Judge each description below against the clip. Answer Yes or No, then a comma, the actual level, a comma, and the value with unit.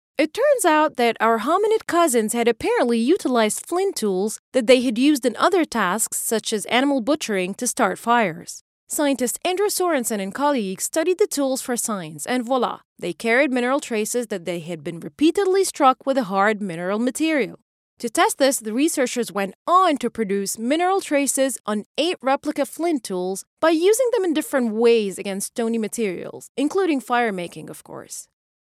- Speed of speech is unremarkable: Yes, average, 175 wpm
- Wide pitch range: Yes, wide, 6.1 semitones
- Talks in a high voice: Yes, very high, 250 Hz